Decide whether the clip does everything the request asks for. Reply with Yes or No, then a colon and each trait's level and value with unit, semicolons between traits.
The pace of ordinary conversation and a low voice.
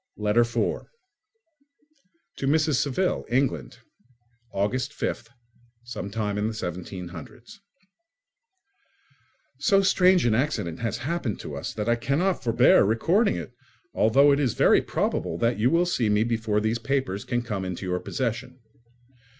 No: slow, 125 wpm; low, 115 Hz